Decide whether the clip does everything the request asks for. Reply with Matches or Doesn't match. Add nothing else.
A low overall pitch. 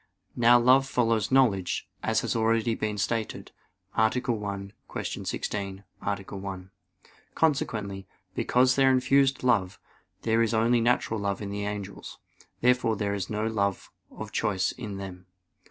Matches